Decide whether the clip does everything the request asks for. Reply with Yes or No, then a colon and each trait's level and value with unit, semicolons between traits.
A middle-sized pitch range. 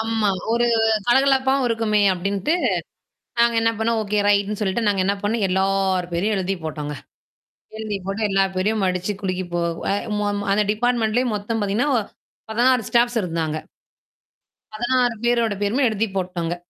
Yes: average, 3.4 semitones